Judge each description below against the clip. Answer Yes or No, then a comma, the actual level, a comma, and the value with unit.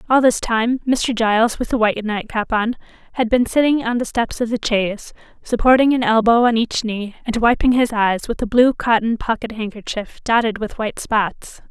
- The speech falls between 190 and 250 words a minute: Yes, average, 200 wpm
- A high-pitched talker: Yes, high, 230 Hz